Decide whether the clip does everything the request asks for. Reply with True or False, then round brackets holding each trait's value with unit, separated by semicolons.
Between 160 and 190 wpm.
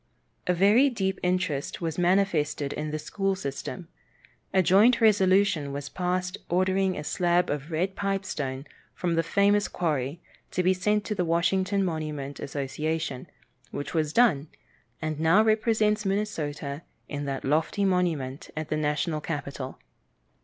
False (140 wpm)